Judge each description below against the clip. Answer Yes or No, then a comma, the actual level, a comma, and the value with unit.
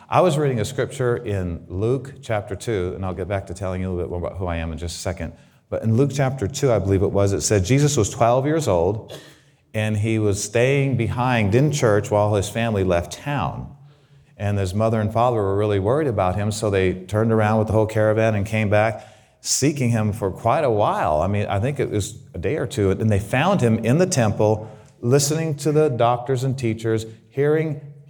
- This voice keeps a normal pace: No, fast, 230 wpm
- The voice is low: Yes, low, 110 Hz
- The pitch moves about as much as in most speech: Yes, average, 4.5 semitones